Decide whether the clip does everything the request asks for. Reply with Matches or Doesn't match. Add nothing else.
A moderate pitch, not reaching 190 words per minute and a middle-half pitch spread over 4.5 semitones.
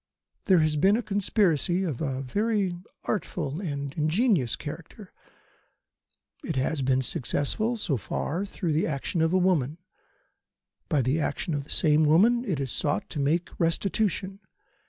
Matches